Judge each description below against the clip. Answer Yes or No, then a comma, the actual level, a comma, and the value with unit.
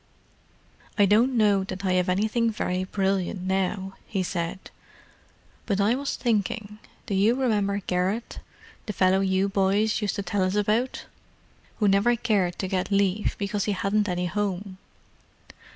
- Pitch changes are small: Yes, narrow, 2.0 semitones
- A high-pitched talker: Yes, high, 200 Hz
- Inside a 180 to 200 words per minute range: No, average, 150 wpm